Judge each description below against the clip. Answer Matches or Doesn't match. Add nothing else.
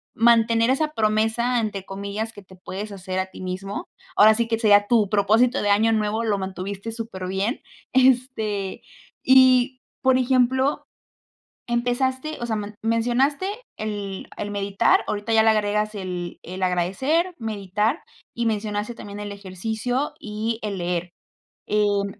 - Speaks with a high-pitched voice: Matches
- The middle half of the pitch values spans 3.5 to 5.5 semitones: Doesn't match